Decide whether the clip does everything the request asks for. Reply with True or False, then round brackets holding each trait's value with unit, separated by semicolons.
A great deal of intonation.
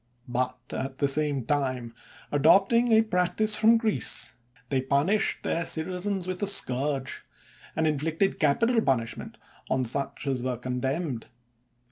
True (6.6 semitones)